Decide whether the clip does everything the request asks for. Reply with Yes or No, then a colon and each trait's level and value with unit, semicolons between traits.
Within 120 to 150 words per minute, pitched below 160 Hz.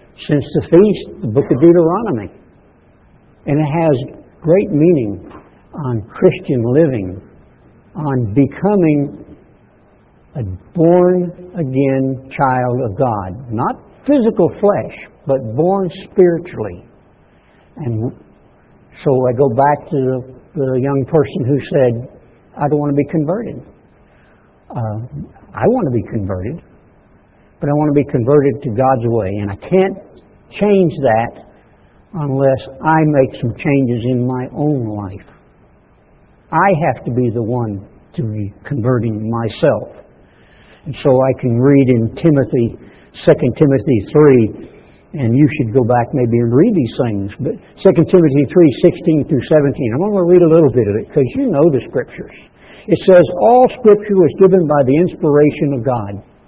Yes: average, 145 wpm; medium, 140 Hz